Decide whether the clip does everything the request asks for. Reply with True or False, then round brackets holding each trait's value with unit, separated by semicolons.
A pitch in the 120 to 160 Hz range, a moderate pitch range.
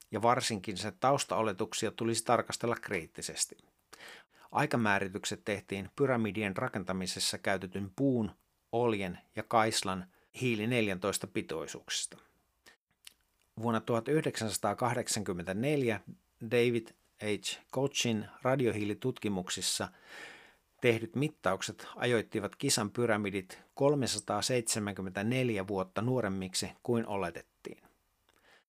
False (110 Hz; 3.2 semitones)